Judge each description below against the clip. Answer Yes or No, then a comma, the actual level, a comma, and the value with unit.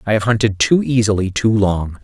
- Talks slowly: No, fast, 205 wpm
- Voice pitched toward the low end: Yes, low, 105 Hz